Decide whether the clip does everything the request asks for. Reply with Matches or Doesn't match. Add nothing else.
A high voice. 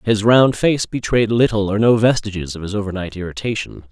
Doesn't match